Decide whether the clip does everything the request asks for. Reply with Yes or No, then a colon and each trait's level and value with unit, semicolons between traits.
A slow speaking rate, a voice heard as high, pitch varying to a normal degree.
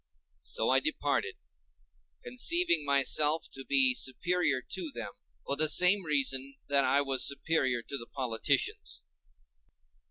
No: slow, 125 wpm; medium, 140 Hz; average, 3.5 semitones